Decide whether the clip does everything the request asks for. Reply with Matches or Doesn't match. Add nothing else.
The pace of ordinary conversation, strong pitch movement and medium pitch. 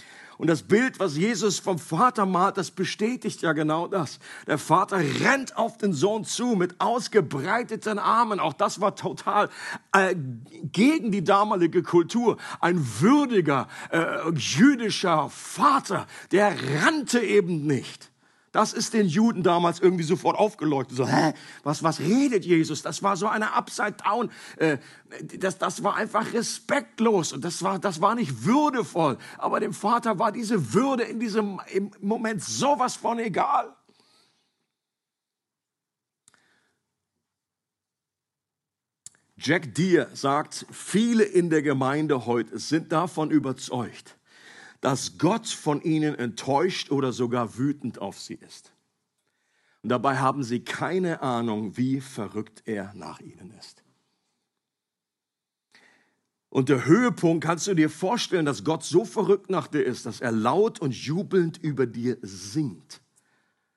Matches